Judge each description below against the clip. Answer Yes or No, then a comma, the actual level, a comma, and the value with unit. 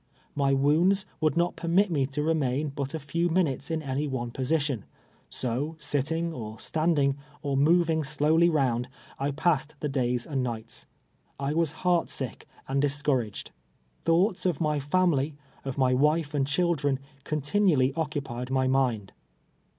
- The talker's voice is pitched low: No, medium, 145 Hz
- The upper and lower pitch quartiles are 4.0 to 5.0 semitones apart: No, average, 3.3 semitones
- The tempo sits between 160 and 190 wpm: Yes, average, 165 wpm